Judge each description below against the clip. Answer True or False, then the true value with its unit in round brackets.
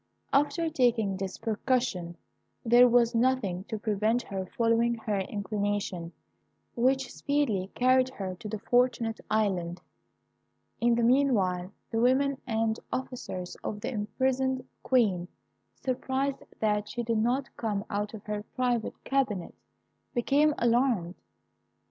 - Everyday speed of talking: False (125 wpm)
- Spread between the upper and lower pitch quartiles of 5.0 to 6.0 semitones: False (3.9 semitones)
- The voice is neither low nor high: False (230 Hz)